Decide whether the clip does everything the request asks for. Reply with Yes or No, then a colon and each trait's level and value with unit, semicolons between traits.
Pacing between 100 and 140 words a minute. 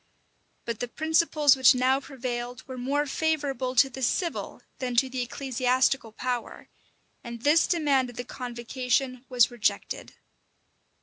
Yes: slow, 135 wpm